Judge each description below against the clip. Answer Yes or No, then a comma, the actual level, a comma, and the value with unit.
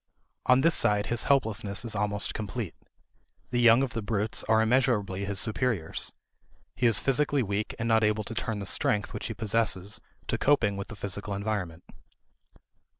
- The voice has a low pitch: Yes, low, 110 Hz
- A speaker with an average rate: Yes, average, 170 wpm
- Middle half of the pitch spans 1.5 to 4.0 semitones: Yes, narrow, 2.6 semitones